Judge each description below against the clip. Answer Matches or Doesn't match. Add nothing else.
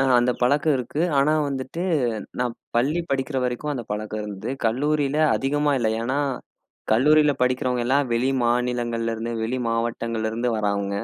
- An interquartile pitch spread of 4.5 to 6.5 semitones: Doesn't match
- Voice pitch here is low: Matches